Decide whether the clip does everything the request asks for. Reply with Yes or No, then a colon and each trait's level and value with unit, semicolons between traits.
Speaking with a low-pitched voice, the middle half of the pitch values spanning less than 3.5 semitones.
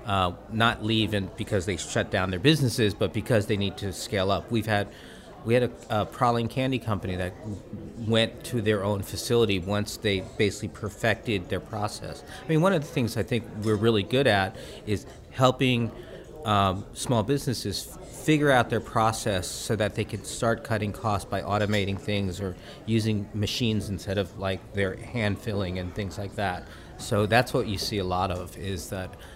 Yes: low, 105 Hz; average, 2.9 semitones